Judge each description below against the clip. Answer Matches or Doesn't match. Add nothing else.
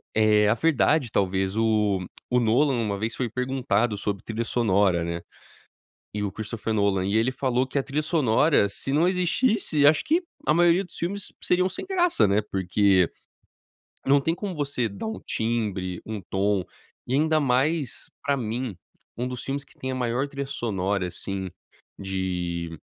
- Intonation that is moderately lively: Doesn't match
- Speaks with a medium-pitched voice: Doesn't match